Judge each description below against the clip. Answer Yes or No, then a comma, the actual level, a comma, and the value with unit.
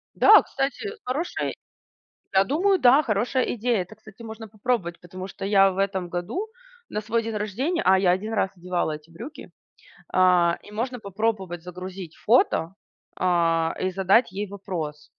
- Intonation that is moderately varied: Yes, average, 4.3 semitones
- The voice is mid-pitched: No, high, 195 Hz